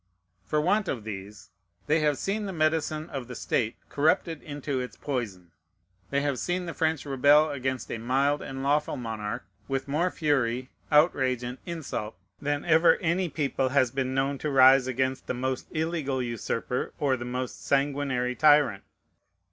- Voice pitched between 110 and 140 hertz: Yes, low, 135 Hz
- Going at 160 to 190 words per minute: Yes, average, 165 wpm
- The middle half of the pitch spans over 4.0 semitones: No, average, 3.3 semitones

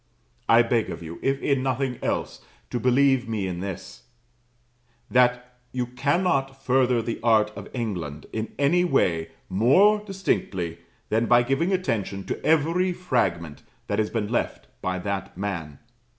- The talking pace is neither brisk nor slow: Yes, average, 150 wpm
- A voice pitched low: Yes, low, 120 Hz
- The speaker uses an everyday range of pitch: No, wide, 5.7 semitones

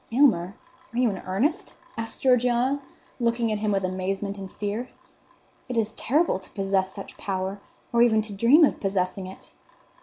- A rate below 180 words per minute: Yes, average, 170 wpm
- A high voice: Yes, high, 215 Hz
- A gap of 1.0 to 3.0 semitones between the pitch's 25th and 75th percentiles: No, average, 3.8 semitones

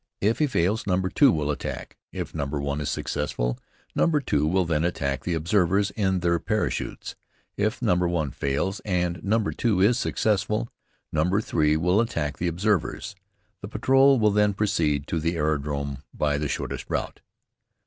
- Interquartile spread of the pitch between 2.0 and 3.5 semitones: No, wide, 5.5 semitones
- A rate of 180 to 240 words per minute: No, average, 165 wpm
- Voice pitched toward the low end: Yes, very low, 90 Hz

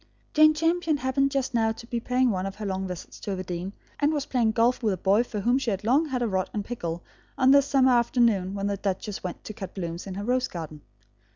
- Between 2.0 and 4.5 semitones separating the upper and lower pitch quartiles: No, average, 5.2 semitones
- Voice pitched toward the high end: Yes, high, 225 Hz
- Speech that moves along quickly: Yes, fast, 250 wpm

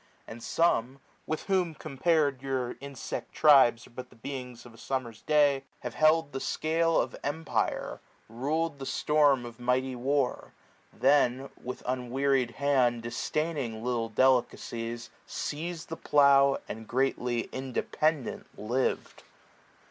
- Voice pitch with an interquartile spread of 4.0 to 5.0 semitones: No, average, 3.2 semitones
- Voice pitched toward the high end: No, low, 135 Hz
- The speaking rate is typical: No, slow, 130 wpm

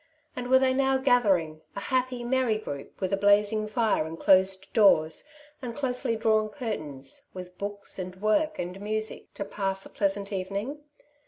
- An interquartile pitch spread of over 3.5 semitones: Yes, average, 4.5 semitones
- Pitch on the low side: No, high, 205 Hz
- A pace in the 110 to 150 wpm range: No, average, 170 wpm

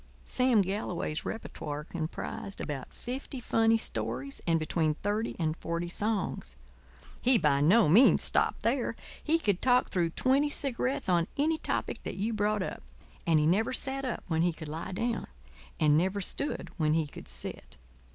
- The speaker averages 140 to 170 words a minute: Yes, average, 165 wpm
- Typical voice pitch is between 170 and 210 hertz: Yes, high, 190 Hz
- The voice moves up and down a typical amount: No, wide, 6.8 semitones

